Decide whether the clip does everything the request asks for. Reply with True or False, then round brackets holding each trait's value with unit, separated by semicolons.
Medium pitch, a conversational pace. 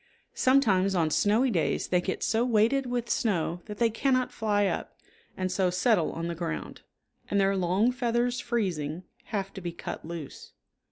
False (200 Hz; 170 wpm)